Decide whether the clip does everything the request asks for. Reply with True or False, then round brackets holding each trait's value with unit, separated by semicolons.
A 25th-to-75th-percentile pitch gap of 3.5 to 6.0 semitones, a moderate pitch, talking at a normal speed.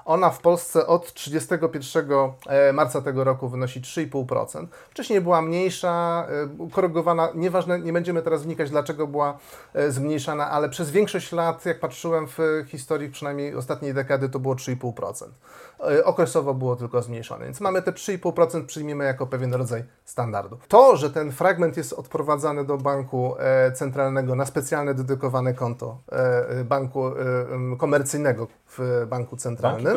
True (4.1 semitones; 145 Hz; 135 wpm)